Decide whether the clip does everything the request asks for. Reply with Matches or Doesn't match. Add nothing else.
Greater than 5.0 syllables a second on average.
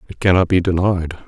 Matches